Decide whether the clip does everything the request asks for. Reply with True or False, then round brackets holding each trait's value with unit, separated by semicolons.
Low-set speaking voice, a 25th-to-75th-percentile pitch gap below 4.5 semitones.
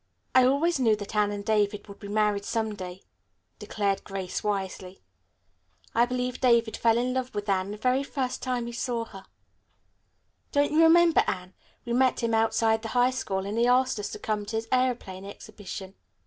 False (225 Hz; 3.7 semitones)